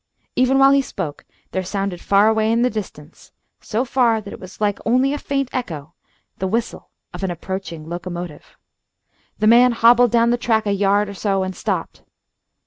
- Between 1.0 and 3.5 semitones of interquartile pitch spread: No, average, 4.2 semitones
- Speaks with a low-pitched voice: No, high, 210 Hz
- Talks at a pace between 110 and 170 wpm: No, average, 185 wpm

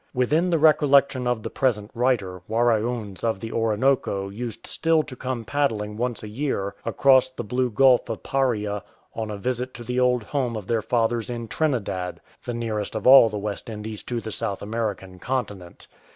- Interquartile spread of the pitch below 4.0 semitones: Yes, average, 3.4 semitones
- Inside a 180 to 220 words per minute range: Yes, average, 185 wpm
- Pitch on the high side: No, low, 115 Hz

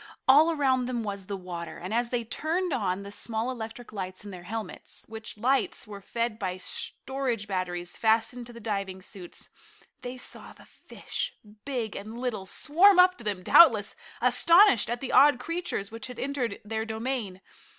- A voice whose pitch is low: No, high, 225 Hz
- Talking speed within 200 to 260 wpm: No, average, 175 wpm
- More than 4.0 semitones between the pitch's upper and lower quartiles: Yes, average, 4.4 semitones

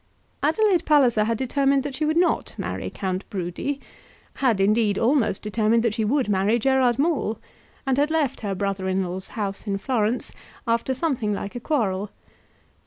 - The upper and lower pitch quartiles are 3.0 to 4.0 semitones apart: No, average, 5.2 semitones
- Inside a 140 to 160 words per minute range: No, average, 170 wpm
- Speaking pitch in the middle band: No, high, 230 Hz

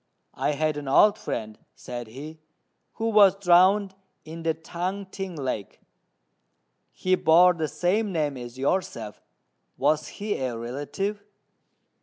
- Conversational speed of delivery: No, slow, 130 wpm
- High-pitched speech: No, medium, 160 Hz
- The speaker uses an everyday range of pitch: No, wide, 6.0 semitones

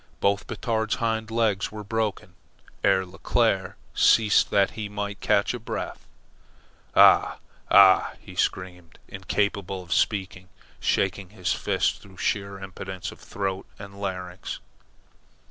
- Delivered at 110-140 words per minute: Yes, slow, 135 wpm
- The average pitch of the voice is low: Yes, low, 100 Hz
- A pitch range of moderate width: No, narrow, 1.9 semitones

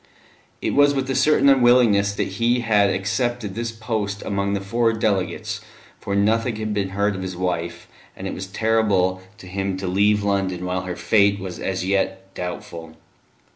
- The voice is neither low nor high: No, low, 100 Hz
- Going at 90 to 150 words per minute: No, average, 175 wpm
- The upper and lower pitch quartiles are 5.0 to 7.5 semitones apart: No, average, 3.0 semitones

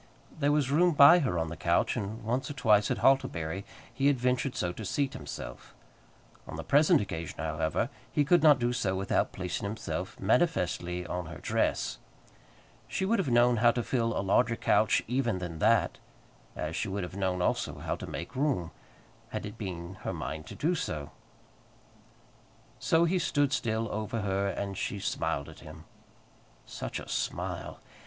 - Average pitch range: No, wide, 7.2 semitones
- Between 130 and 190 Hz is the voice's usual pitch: No, low, 110 Hz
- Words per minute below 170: No, average, 175 wpm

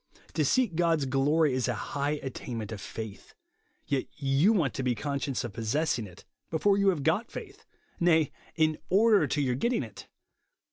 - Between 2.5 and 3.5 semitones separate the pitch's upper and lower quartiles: No, wide, 5.4 semitones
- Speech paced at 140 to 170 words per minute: No, average, 190 wpm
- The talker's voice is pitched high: No, medium, 145 Hz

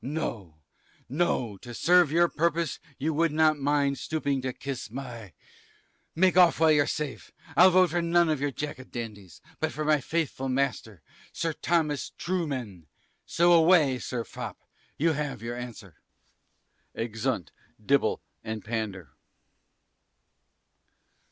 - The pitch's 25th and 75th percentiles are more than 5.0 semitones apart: Yes, wide, 5.4 semitones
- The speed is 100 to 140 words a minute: Yes, slow, 135 wpm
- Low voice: No, medium, 145 Hz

